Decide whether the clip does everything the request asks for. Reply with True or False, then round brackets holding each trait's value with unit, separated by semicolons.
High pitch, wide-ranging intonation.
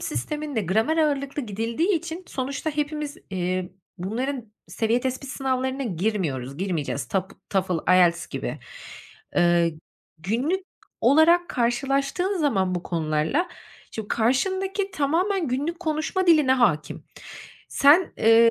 True (260 Hz; 8.3 semitones)